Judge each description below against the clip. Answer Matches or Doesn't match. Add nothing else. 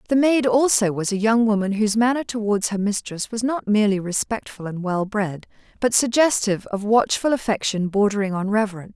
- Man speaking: Doesn't match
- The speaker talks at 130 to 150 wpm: Doesn't match